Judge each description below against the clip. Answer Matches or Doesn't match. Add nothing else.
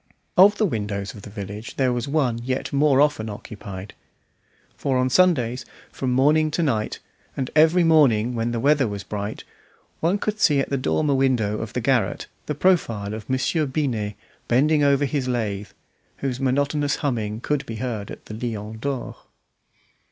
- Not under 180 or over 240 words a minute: Doesn't match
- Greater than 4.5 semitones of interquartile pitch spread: Matches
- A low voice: Matches